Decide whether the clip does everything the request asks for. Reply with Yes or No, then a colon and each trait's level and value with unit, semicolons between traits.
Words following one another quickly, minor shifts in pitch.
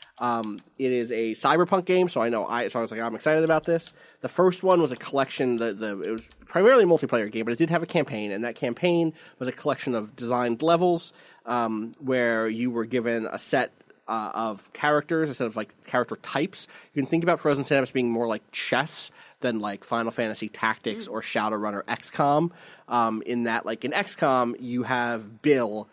No: fast, 210 wpm; average, 5.0 semitones